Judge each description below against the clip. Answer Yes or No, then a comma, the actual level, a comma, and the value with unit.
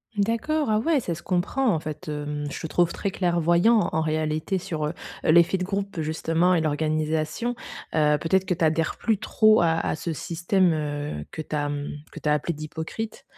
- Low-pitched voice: No, medium, 165 Hz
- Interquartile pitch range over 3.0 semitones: Yes, average, 3.7 semitones